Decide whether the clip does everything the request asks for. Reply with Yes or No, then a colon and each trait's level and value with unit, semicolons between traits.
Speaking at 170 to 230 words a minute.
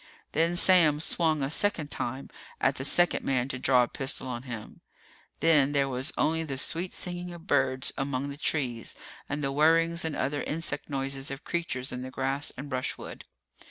Yes: average, 185 wpm